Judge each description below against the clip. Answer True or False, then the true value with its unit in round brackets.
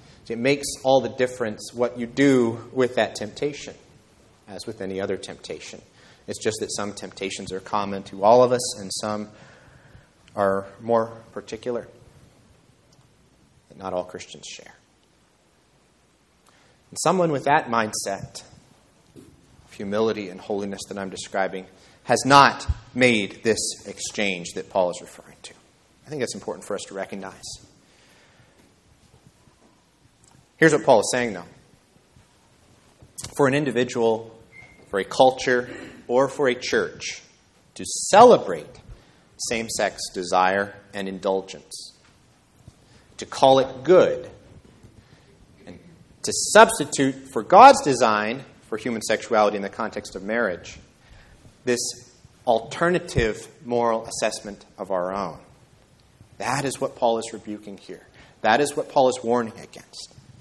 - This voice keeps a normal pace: False (125 wpm)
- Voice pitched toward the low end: True (115 Hz)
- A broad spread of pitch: False (4.3 semitones)